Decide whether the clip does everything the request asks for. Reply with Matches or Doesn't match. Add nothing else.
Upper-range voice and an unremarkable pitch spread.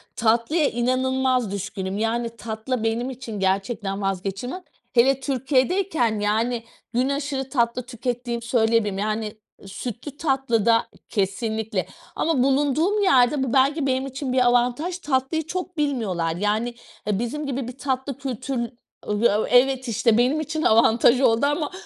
Matches